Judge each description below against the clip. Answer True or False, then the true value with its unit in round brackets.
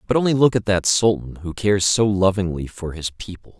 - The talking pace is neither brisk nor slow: False (215 wpm)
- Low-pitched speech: True (100 Hz)